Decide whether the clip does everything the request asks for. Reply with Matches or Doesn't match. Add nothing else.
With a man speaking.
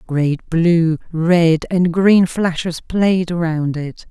Doesn't match